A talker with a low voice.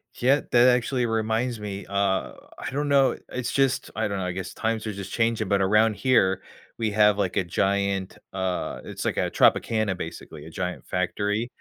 Yes: low, 105 Hz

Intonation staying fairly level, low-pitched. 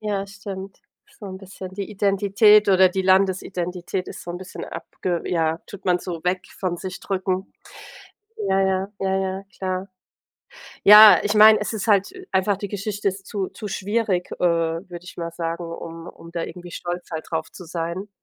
No: narrow, 2.1 semitones; high, 190 Hz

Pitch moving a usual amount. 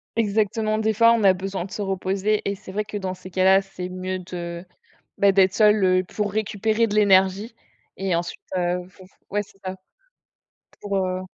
No: narrow, 2.1 semitones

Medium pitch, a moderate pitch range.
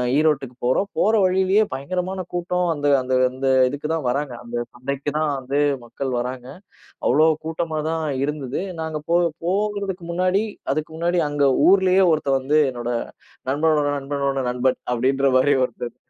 Yes: medium, 145 Hz; average, 4.6 semitones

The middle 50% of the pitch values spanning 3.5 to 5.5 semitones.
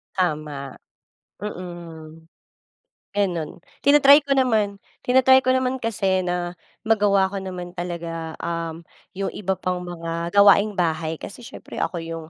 Yes: average, 3.8 semitones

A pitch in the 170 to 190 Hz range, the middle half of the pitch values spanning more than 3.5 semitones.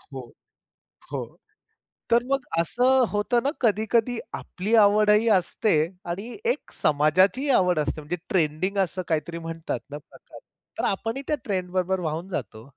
Yes: medium, 185 Hz; wide, 5.4 semitones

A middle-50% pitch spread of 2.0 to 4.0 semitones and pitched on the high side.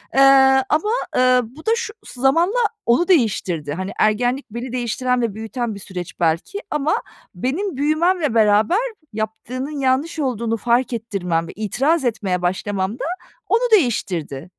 No: wide, 5.6 semitones; high, 245 Hz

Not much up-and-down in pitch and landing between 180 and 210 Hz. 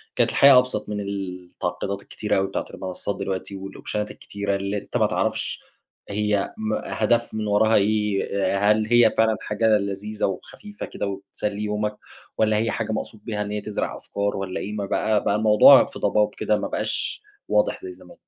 No: narrow, 1.4 semitones; low, 105 Hz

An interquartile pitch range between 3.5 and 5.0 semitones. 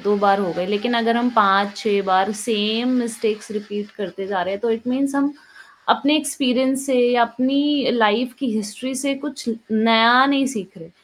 Yes: average, 4.0 semitones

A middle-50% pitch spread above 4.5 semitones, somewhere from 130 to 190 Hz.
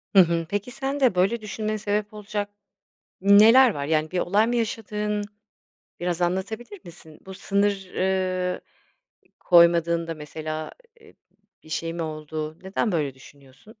No: average, 4.2 semitones; medium, 185 Hz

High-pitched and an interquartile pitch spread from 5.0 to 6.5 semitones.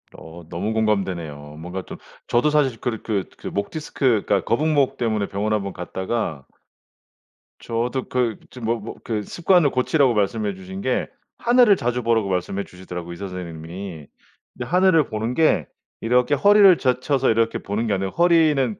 No: low, 110 Hz; wide, 5.4 semitones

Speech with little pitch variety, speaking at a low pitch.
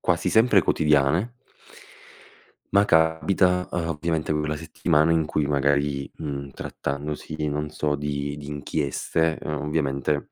Yes: narrow, 2.0 semitones; very low, 75 Hz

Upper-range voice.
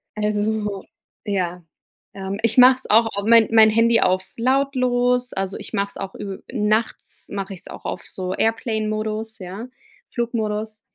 Yes: high, 215 Hz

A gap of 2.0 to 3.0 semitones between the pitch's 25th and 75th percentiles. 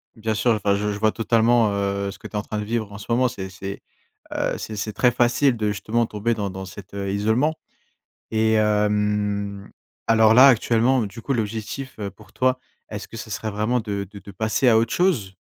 Yes: narrow, 2.4 semitones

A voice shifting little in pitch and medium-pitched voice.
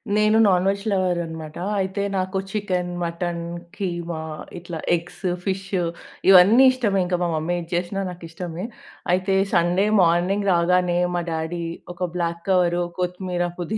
Yes: narrow, 1.8 semitones; medium, 180 Hz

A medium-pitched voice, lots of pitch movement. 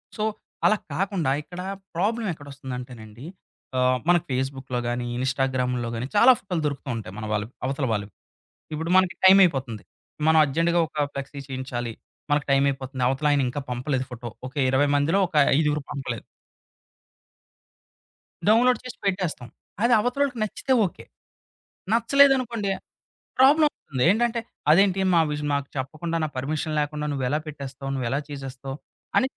Yes: medium, 145 Hz; wide, 6.0 semitones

